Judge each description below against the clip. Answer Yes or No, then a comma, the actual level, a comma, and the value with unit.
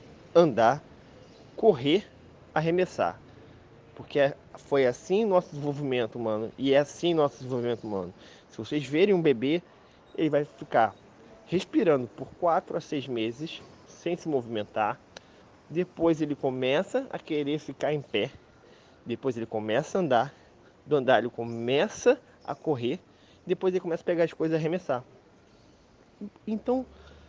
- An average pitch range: No, wide, 5.9 semitones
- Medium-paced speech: Yes, average, 135 wpm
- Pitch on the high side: No, medium, 145 Hz